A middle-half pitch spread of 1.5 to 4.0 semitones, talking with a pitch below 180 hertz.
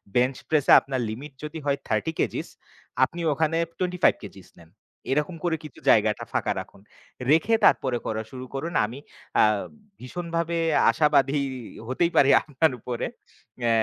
No: average, 4.7 semitones; medium, 140 Hz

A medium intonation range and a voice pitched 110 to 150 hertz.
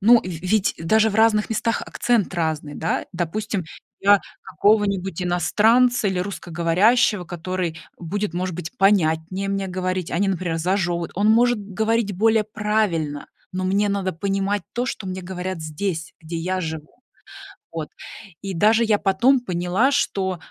No: average, 3.4 semitones; high, 190 Hz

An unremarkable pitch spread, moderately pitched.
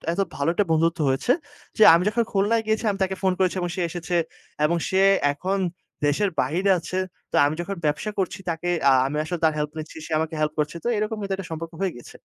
Yes: average, 3.6 semitones; medium, 175 Hz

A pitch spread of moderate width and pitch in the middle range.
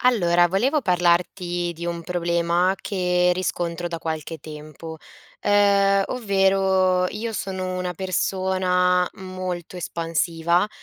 No: narrow, 1.8 semitones; medium, 180 Hz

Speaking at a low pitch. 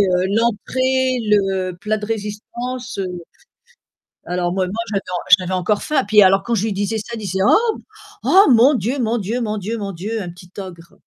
No: high, 210 Hz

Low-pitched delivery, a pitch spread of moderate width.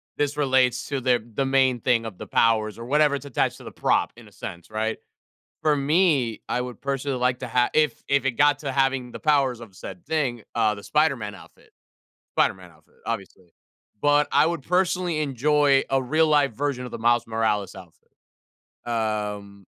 Yes: low, 125 Hz; average, 4.3 semitones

